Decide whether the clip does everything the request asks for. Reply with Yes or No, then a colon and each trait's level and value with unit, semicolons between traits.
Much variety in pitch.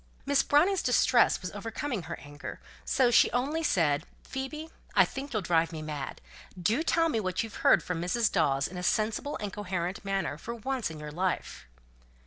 Yes: wide, 7.6 semitones